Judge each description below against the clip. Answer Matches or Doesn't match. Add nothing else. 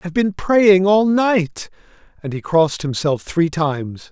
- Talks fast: Doesn't match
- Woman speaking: Doesn't match